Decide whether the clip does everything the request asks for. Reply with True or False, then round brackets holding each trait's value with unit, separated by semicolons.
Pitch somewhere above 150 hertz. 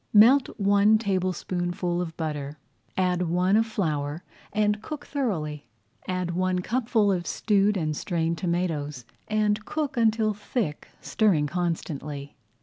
True (185 Hz)